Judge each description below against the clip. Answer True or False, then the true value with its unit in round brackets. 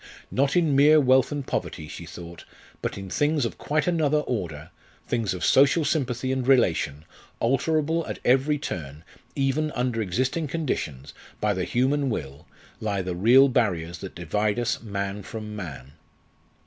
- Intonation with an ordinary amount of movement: False (7.4 semitones)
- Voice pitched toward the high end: False (120 Hz)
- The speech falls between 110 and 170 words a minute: True (155 wpm)